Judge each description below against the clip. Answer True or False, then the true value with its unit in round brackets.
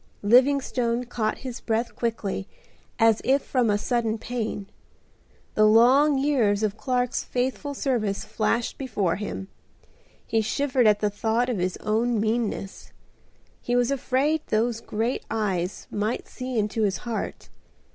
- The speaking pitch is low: False (230 Hz)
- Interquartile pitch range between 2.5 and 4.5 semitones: True (2.9 semitones)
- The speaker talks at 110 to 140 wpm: True (135 wpm)